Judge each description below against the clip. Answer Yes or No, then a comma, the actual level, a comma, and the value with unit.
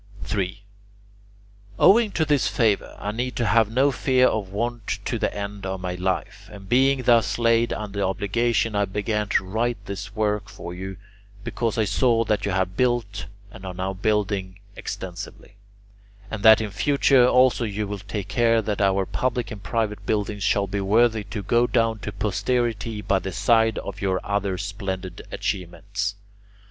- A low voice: Yes, low, 105 Hz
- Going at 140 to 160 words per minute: No, average, 170 wpm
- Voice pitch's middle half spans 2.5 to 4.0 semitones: Yes, average, 2.9 semitones